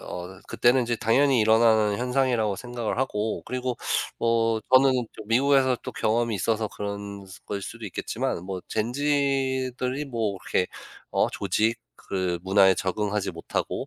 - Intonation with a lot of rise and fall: No, average, 3.8 semitones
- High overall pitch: No, low, 115 Hz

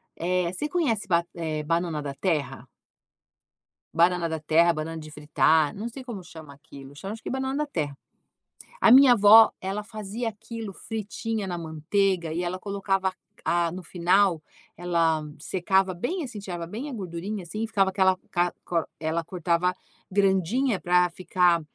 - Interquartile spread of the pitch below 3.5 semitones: No, average, 3.8 semitones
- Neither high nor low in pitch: Yes, medium, 180 Hz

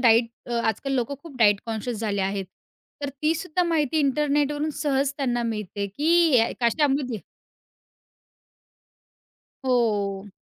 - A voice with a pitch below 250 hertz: No, very high, 255 Hz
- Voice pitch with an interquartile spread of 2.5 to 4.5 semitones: No, average, 5.1 semitones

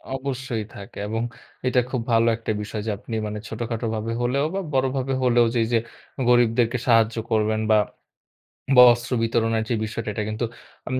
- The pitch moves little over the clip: Yes, narrow, 2.1 semitones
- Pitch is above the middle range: No, low, 115 Hz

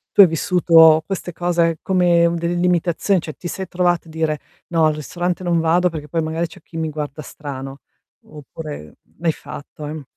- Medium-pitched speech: Yes, medium, 165 Hz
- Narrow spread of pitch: Yes, narrow, 2.1 semitones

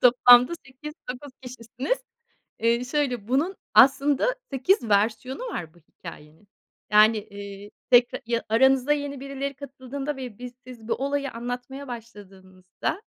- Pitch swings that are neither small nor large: Yes, average, 3.8 semitones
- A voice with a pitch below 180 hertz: No, very high, 250 Hz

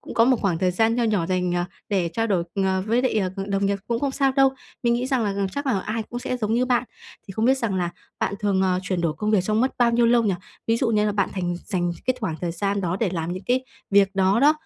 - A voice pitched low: No, high, 210 Hz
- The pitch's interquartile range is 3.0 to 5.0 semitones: Yes, average, 4.2 semitones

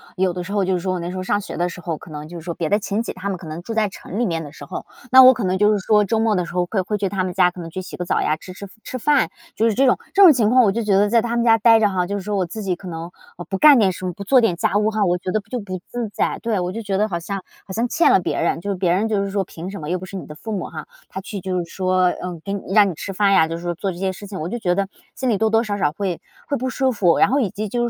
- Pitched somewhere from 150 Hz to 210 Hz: Yes, high, 195 Hz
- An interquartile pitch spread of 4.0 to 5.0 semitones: No, average, 3.4 semitones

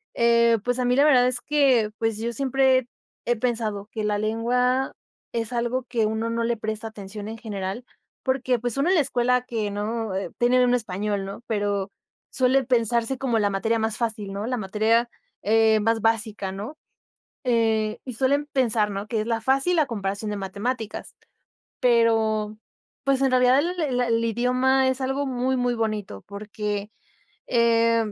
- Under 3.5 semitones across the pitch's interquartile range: Yes, average, 2.8 semitones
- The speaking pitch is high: Yes, high, 230 Hz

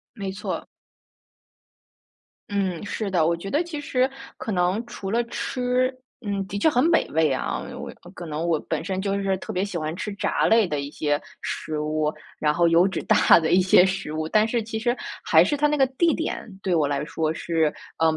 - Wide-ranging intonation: Yes, wide, 6.2 semitones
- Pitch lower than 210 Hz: Yes, high, 190 Hz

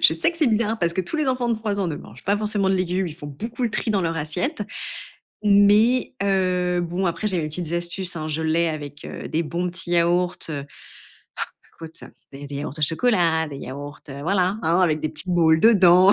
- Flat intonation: No, average, 4.1 semitones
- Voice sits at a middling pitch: Yes, medium, 180 Hz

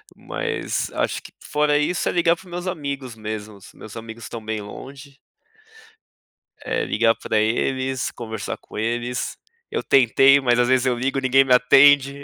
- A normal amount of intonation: Yes, average, 3.5 semitones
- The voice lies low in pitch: Yes, low, 130 Hz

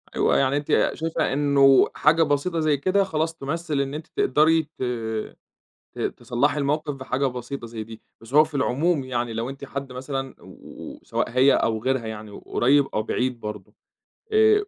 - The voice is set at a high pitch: No, medium, 140 Hz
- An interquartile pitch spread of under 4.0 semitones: Yes, average, 3.4 semitones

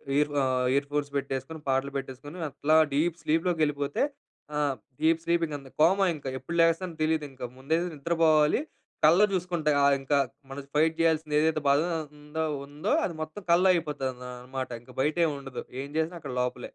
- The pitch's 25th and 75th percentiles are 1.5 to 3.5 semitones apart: Yes, average, 2.8 semitones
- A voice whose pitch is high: No, medium, 150 Hz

